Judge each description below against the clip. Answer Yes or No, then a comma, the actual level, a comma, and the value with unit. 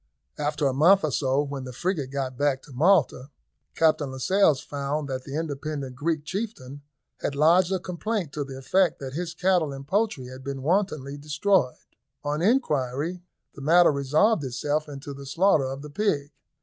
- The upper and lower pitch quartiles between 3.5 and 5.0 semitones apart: Yes, average, 4.2 semitones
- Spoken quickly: No, average, 175 wpm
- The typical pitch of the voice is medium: Yes, medium, 145 Hz